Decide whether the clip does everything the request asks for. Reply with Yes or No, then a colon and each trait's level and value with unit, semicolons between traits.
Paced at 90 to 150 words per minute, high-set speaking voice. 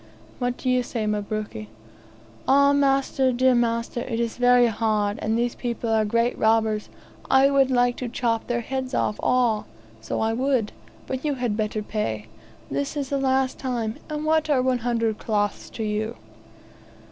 No: average, 170 wpm; high, 240 Hz